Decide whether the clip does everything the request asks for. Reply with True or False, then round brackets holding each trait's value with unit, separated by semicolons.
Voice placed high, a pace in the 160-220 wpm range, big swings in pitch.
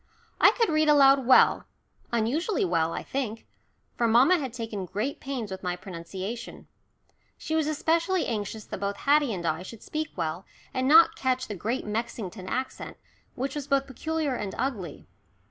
True (240 Hz; 165 wpm; 6.1 semitones)